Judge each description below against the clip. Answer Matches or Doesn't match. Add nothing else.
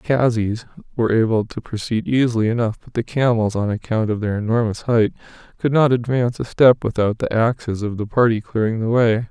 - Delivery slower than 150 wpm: Doesn't match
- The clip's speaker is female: Doesn't match